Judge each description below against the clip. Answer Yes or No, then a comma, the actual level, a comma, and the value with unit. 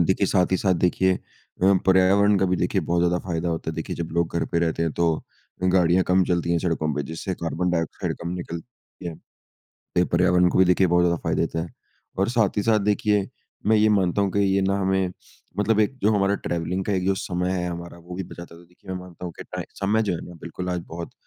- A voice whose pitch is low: Yes, very low, 90 Hz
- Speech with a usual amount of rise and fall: No, narrow, 2.1 semitones